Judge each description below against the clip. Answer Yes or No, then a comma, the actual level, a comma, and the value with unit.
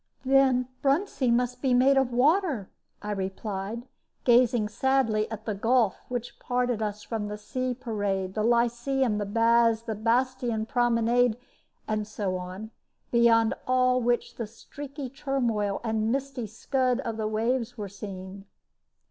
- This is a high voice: Yes, high, 235 Hz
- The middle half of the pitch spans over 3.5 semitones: No, average, 2.9 semitones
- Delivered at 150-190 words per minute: No, average, 140 wpm